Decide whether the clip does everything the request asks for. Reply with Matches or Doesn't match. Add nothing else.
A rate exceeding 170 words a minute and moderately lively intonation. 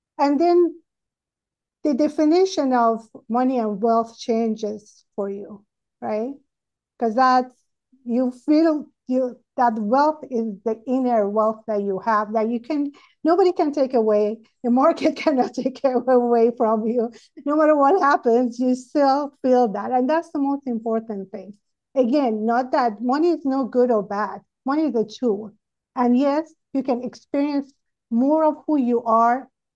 Doesn't match